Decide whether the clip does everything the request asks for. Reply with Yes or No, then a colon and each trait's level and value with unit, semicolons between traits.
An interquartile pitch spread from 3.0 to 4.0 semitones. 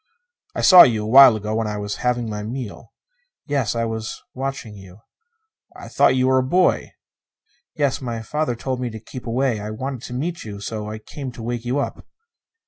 Yes: average, 3.3 semitones